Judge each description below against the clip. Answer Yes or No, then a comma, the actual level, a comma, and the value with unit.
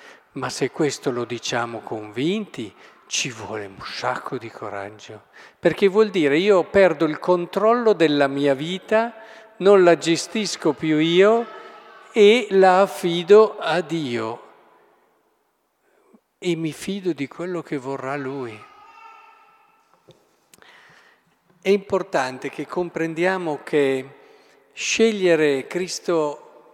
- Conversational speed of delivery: No, slow, 105 wpm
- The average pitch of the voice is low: No, medium, 180 Hz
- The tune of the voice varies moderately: No, wide, 6.3 semitones